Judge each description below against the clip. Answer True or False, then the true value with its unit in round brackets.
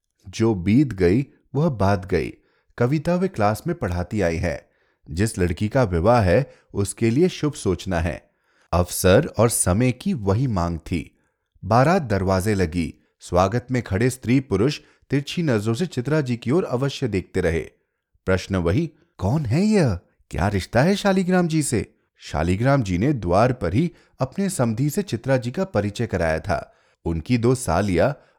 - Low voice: True (115 Hz)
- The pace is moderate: True (160 wpm)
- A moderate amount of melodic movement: False (7.4 semitones)